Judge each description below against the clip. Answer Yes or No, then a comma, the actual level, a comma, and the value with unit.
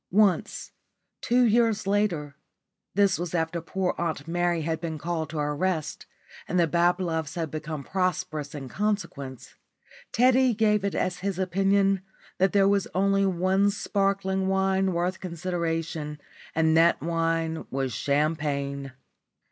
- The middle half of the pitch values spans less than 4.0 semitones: Yes, average, 3.4 semitones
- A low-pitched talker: No, medium, 175 Hz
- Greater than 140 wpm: No, slow, 135 wpm